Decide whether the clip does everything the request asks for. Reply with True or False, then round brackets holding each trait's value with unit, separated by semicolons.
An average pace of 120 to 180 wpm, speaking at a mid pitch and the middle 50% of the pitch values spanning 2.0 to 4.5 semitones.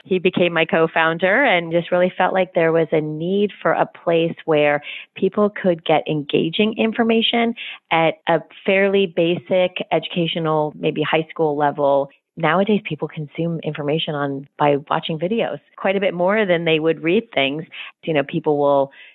True (165 wpm; 165 Hz; 3.3 semitones)